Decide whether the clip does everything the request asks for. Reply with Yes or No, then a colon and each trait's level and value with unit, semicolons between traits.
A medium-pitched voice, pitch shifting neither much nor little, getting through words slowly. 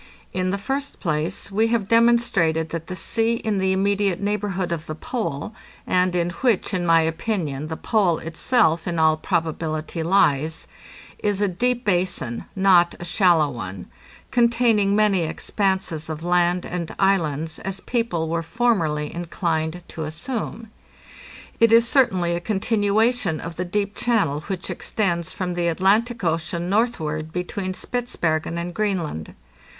No: medium, 180 Hz; average, 4.4 semitones; average, 145 wpm